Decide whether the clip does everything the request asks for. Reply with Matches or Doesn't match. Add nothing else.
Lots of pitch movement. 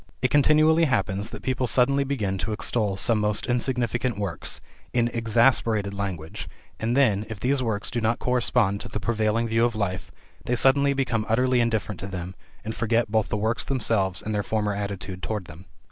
Doesn't match